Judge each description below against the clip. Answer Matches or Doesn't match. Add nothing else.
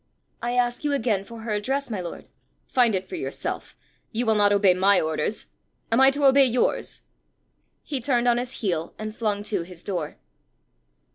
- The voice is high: Matches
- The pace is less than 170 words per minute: Doesn't match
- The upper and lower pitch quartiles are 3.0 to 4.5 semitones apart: Matches